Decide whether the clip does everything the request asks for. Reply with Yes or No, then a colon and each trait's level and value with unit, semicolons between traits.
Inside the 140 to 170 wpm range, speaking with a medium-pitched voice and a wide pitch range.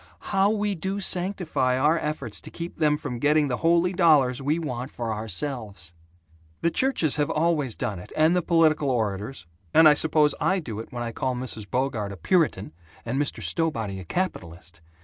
No: average, 185 wpm; medium, 145 Hz; wide, 6.4 semitones